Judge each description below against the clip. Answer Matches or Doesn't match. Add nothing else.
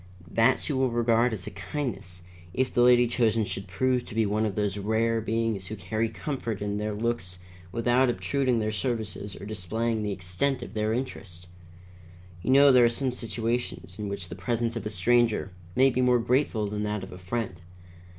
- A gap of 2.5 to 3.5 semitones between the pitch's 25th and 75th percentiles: Matches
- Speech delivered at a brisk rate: Doesn't match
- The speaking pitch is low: Matches